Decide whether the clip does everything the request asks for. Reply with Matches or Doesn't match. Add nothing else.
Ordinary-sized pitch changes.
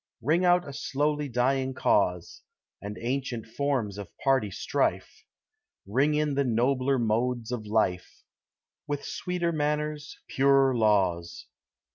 Matches